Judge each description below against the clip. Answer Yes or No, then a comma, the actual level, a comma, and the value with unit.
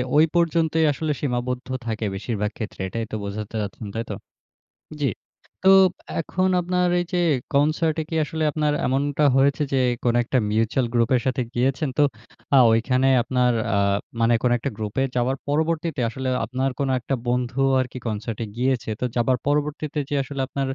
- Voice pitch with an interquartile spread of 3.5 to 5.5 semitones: Yes, average, 3.9 semitones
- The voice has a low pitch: Yes, low, 130 Hz